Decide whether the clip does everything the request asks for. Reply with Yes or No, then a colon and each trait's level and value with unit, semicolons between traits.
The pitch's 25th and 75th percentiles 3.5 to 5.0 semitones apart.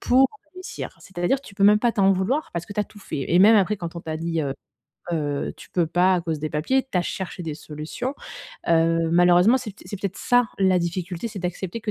Yes: average, 4.0 semitones